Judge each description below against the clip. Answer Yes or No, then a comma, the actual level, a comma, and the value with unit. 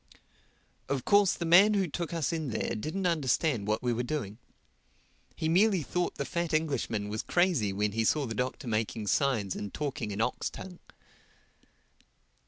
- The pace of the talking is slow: No, average, 170 wpm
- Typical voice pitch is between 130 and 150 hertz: Yes, medium, 140 Hz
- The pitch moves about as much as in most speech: No, wide, 7.4 semitones